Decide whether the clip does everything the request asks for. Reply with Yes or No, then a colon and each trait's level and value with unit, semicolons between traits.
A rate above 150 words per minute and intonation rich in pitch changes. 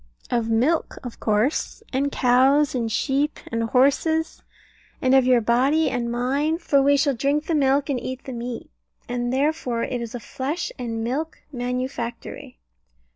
No: average, 160 wpm; average, 2.9 semitones